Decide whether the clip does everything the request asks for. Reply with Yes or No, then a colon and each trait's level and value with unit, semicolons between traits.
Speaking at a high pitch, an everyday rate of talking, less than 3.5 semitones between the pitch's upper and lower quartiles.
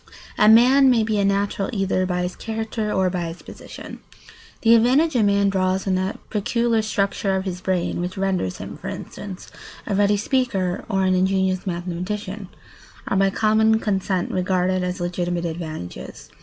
Yes: high, 195 Hz; average, 170 wpm; average, 2.7 semitones